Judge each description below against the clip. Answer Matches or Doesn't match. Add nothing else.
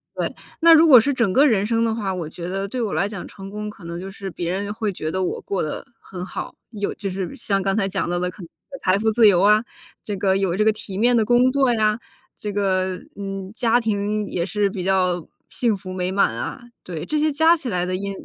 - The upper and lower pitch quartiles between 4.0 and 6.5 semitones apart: Doesn't match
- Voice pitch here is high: Matches